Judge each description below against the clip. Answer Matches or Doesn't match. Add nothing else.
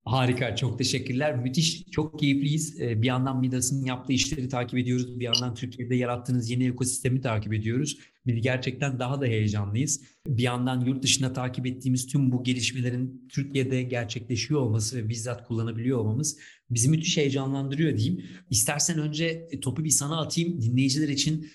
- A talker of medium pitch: Doesn't match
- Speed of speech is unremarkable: Doesn't match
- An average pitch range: Doesn't match